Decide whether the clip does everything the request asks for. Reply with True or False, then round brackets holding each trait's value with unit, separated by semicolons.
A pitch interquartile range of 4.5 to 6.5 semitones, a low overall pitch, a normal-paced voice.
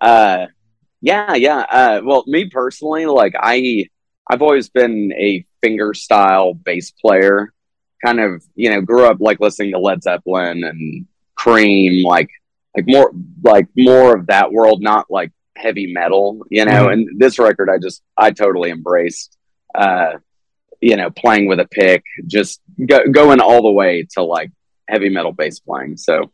True (5.0 semitones; 110 Hz; 165 wpm)